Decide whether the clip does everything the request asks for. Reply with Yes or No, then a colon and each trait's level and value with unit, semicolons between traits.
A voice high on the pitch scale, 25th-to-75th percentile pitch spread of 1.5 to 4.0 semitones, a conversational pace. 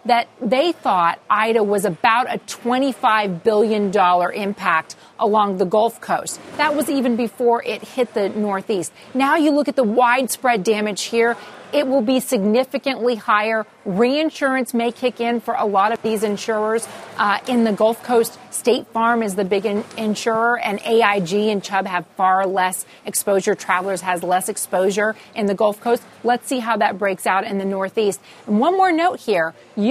Yes: high, 220 Hz; average, 3.2 semitones; average, 175 wpm